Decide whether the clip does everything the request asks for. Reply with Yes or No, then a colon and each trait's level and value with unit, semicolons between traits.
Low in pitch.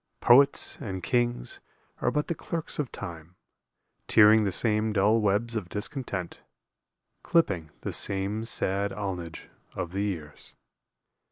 Yes: low, 105 Hz